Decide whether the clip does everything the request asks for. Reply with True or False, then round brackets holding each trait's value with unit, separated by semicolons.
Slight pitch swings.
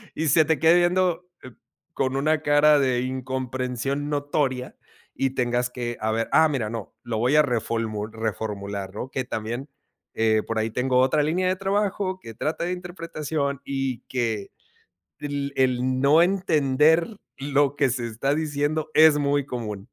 False (4.2 semitones)